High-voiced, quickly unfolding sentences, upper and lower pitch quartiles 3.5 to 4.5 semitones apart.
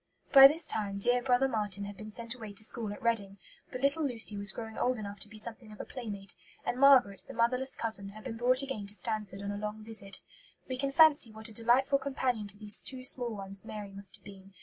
Yes: high, 220 Hz; fast, 240 wpm; average, 3.8 semitones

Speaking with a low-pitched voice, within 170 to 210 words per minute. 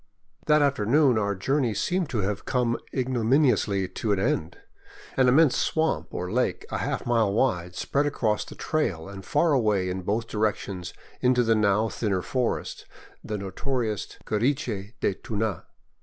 No: low, 110 Hz; average, 155 wpm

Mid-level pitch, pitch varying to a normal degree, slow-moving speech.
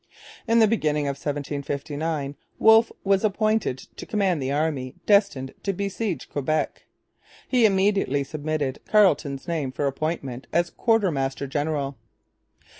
No: medium, 155 Hz; wide, 6.1 semitones; slow, 120 wpm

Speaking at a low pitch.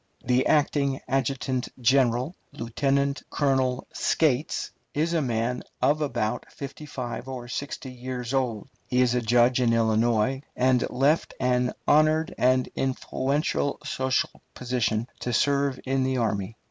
Yes: low, 130 Hz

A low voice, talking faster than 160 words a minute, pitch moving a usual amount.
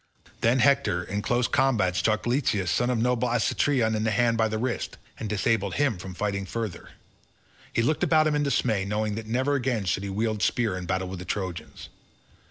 Yes: low, 110 Hz; average, 200 wpm; average, 3.9 semitones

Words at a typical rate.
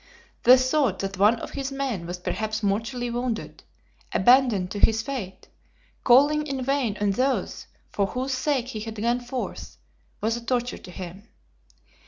Yes: average, 160 wpm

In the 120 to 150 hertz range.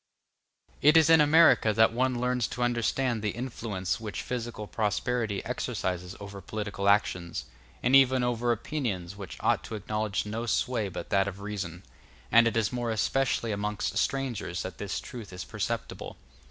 No: low, 110 Hz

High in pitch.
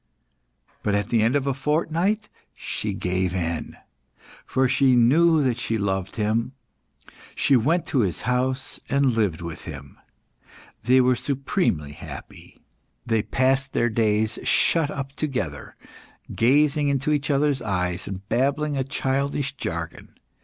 No: low, 130 Hz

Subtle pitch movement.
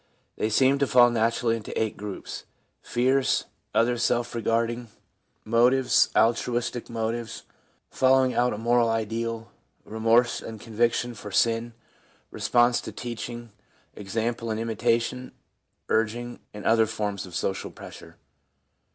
Yes: narrow, 1.3 semitones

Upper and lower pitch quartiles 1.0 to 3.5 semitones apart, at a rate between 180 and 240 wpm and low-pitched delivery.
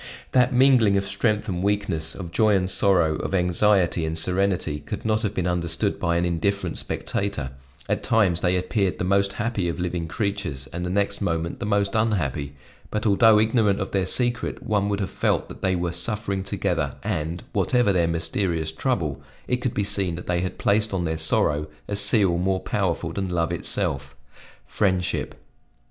Yes: average, 3.2 semitones; average, 185 wpm; very low, 95 Hz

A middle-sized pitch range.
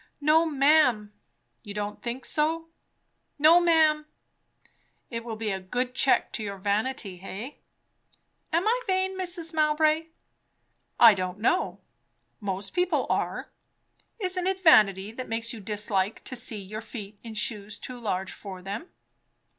No: wide, 7.5 semitones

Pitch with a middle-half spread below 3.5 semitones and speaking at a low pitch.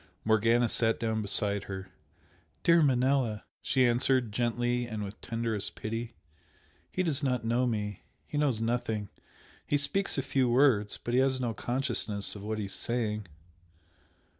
Yes: average, 3.1 semitones; low, 120 Hz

